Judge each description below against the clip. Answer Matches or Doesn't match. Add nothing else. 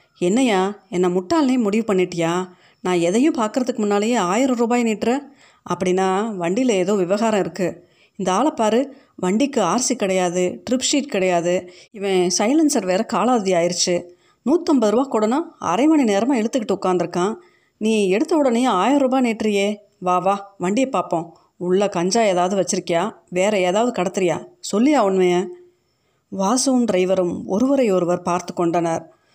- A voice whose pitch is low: Doesn't match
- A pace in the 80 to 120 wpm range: Doesn't match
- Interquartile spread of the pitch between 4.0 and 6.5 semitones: Matches